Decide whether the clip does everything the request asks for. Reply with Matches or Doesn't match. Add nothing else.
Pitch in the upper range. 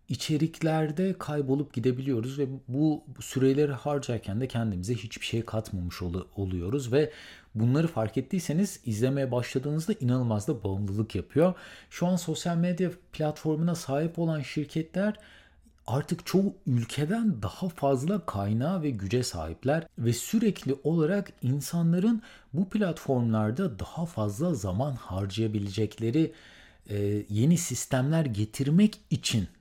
Doesn't match